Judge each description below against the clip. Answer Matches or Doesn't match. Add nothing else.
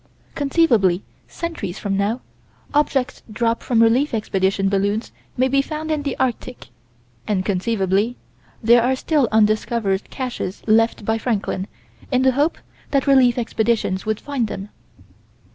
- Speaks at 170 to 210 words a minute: Doesn't match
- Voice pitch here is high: Matches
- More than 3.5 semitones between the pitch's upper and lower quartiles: Matches